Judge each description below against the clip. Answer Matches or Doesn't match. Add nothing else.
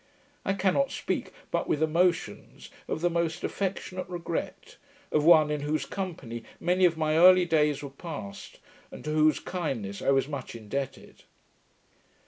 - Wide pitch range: Doesn't match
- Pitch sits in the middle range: Matches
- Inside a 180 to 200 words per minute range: Doesn't match